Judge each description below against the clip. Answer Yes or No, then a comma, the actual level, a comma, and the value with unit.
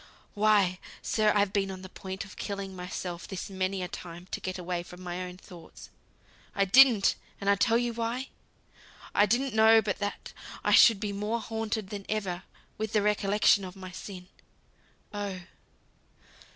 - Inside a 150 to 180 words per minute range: Yes, average, 170 wpm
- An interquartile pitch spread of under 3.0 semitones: Yes, narrow, 2.6 semitones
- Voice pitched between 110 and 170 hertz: No, high, 200 Hz